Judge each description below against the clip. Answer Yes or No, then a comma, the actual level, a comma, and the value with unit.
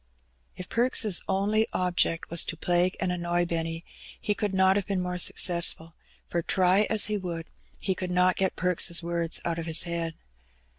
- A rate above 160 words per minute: Yes, average, 180 wpm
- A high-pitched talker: No, medium, 180 Hz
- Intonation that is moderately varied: No, narrow, 2.0 semitones